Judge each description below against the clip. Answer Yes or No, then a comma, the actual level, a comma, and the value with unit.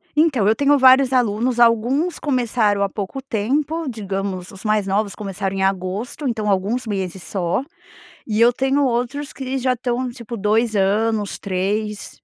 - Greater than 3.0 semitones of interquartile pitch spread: Yes, average, 4.4 semitones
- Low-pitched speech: No, high, 225 Hz